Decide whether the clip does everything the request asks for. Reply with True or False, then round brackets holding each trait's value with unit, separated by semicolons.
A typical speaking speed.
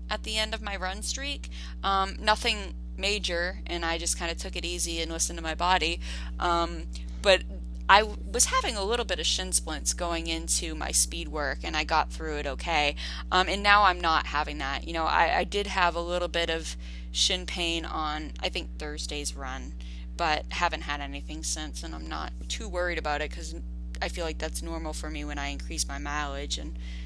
False (210 wpm)